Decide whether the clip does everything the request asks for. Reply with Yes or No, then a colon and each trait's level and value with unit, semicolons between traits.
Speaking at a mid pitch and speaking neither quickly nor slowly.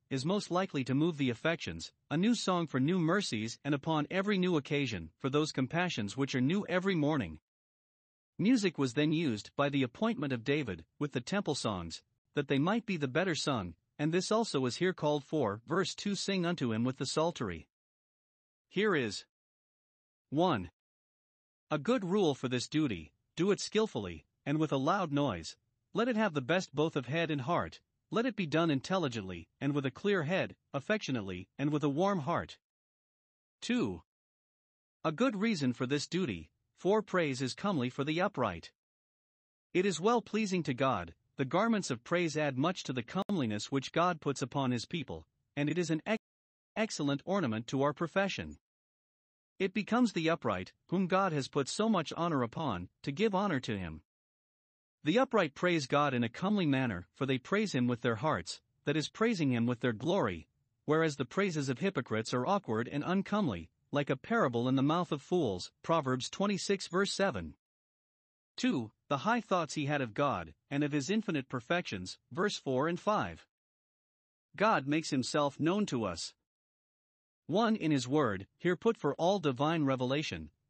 Yes: medium, 150 Hz; average, 180 wpm